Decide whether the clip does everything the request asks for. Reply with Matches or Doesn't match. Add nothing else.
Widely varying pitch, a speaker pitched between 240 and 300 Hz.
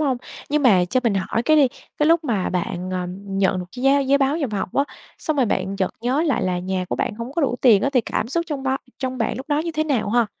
Matches